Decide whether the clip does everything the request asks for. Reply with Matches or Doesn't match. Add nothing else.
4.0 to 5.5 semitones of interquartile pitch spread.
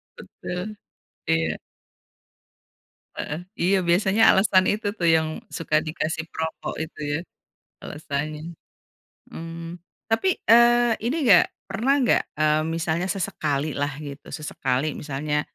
Matches